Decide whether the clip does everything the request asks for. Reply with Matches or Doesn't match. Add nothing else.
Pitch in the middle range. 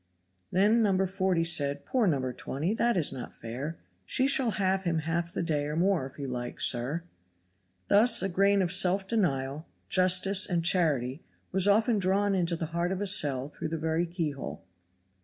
Matches